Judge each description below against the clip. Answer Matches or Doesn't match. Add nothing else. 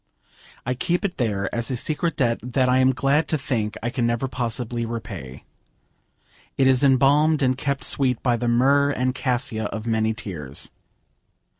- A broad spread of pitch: Doesn't match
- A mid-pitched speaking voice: Doesn't match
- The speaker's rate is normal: Matches